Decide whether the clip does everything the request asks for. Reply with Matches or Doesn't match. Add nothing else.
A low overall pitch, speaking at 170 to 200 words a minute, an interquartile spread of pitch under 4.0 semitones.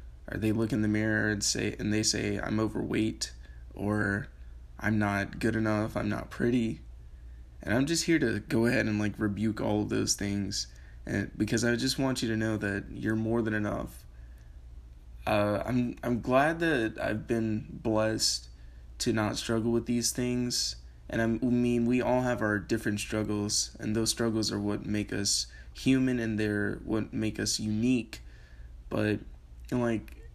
Doesn't match